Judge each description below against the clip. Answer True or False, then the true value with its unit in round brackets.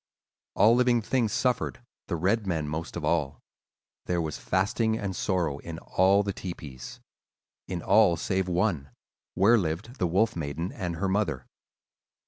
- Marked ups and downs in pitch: False (4.3 semitones)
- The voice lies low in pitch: True (95 Hz)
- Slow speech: False (145 wpm)